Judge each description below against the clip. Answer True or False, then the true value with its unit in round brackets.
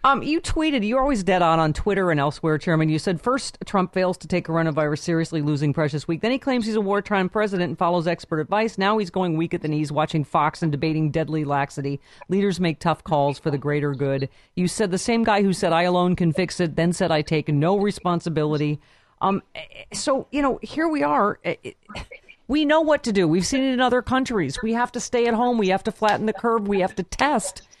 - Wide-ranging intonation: True (6.0 semitones)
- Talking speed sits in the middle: False (235 wpm)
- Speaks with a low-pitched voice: False (185 Hz)